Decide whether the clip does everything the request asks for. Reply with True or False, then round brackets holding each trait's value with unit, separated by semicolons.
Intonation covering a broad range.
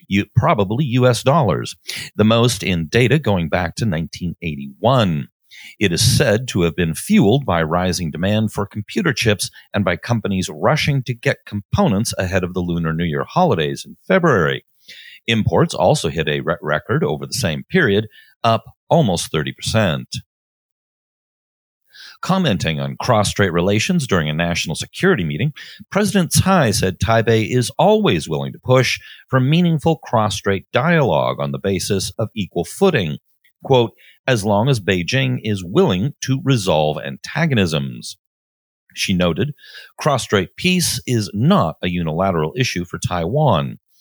True (6.9 semitones)